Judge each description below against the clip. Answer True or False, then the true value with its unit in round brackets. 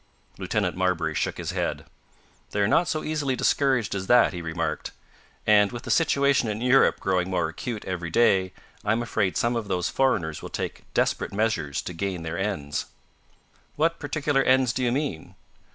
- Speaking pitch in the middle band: False (105 Hz)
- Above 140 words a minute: True (175 wpm)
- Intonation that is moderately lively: False (6.4 semitones)